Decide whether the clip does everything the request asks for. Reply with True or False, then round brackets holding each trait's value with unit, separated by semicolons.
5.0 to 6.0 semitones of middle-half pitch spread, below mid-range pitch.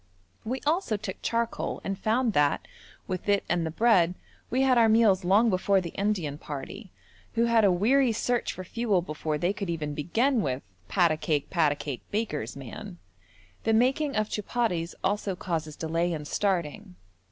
False (5.5 semitones; 195 Hz)